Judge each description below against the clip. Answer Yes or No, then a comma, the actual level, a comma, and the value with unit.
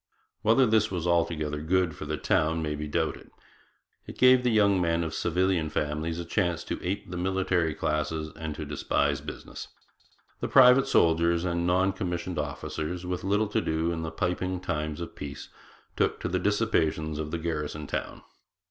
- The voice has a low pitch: Yes, very low, 85 Hz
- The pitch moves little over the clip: No, average, 3.2 semitones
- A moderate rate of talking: Yes, average, 175 wpm